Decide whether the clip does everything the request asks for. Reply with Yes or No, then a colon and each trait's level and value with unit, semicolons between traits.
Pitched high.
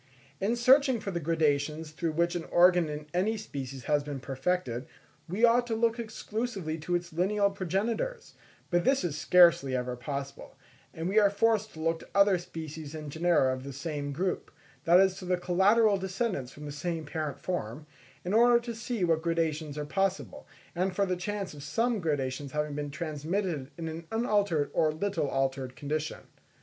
No: medium, 170 Hz